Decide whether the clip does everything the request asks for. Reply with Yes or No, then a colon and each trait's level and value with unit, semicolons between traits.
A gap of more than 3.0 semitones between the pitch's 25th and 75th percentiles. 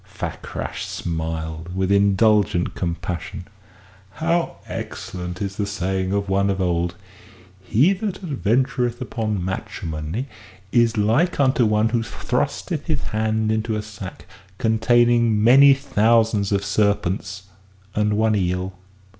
Yes: average, 3.7 semitones